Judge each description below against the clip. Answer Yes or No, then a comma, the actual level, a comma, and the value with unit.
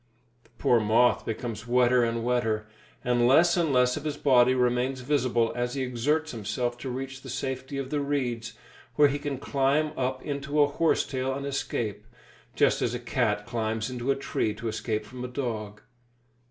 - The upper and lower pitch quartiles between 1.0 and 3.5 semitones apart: Yes, average, 2.8 semitones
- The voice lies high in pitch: No, low, 125 Hz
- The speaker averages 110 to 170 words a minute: No, average, 185 wpm